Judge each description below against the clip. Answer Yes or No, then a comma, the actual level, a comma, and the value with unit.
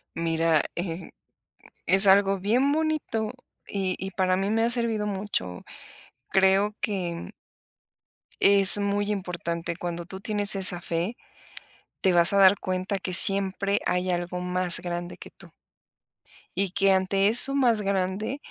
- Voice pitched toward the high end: Yes, high, 195 Hz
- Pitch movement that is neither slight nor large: No, narrow, 2.3 semitones